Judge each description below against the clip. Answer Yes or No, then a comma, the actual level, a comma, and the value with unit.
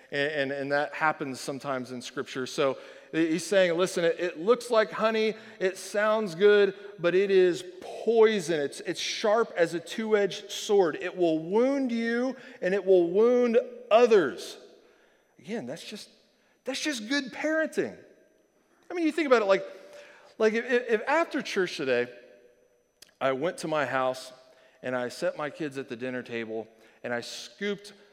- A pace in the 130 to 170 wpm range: Yes, average, 165 wpm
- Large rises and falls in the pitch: Yes, wide, 7.8 semitones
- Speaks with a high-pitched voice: Yes, high, 195 Hz